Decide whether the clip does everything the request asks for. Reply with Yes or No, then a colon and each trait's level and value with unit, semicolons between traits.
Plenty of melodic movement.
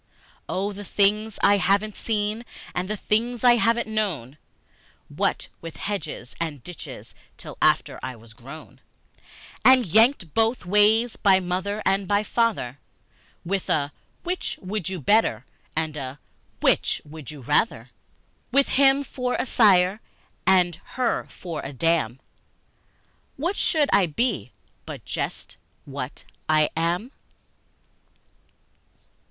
Yes: wide, 6.1 semitones